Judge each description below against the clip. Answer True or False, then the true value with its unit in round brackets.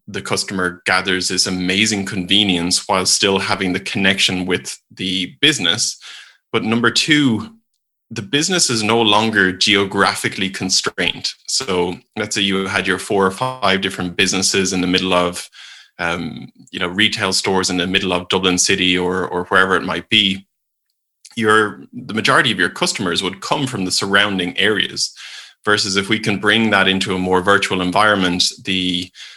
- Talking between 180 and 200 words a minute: False (165 wpm)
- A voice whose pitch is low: True (95 Hz)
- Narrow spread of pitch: True (2.3 semitones)